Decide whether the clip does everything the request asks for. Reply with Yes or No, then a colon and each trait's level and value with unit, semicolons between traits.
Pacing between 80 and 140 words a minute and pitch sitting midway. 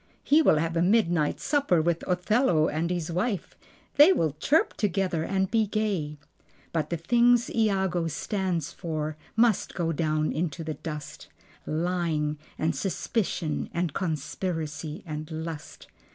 Yes: slow, 135 wpm; medium, 170 Hz